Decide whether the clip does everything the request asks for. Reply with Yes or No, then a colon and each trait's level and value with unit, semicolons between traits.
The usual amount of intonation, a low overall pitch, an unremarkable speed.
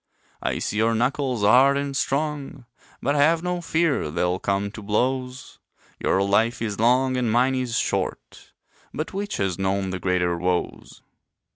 No: wide, 5.8 semitones; low, 120 Hz; average, 155 wpm